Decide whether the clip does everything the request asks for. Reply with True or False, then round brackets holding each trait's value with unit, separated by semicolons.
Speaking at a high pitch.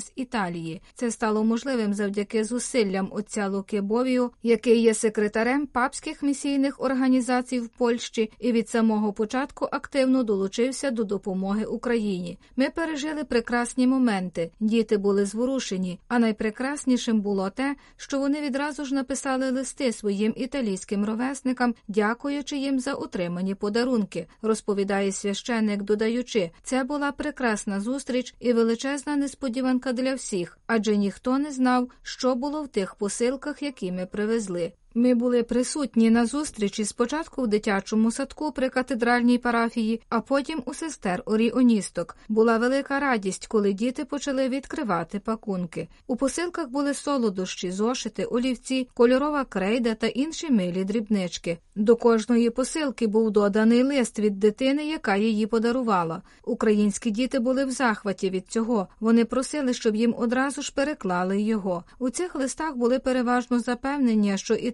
True (235 Hz)